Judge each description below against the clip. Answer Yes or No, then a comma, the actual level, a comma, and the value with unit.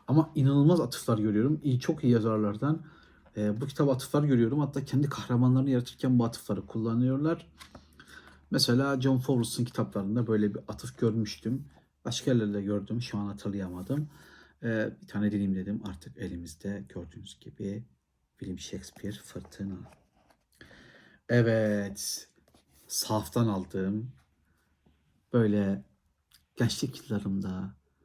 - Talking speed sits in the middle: Yes, average, 110 wpm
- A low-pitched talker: Yes, low, 110 Hz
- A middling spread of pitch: Yes, average, 4.5 semitones